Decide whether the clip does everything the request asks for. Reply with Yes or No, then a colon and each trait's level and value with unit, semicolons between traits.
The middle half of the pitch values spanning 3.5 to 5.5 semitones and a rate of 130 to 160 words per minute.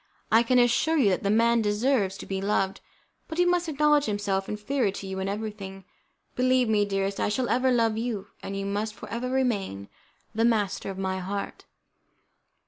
No: average, 4.0 semitones; average, 190 wpm